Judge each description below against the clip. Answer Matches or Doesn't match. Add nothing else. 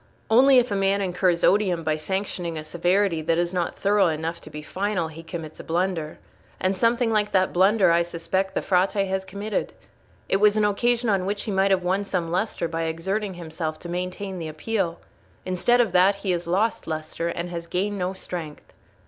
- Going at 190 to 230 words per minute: Matches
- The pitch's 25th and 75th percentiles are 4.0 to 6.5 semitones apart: Doesn't match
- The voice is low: Doesn't match